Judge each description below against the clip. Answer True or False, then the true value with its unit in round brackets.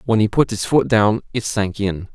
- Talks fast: True (250 wpm)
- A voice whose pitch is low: True (105 Hz)